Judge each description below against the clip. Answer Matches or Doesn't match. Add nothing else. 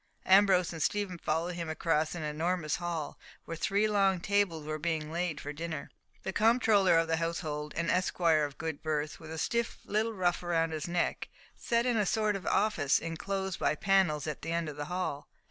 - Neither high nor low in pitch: Matches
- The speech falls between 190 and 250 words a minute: Matches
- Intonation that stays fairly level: Doesn't match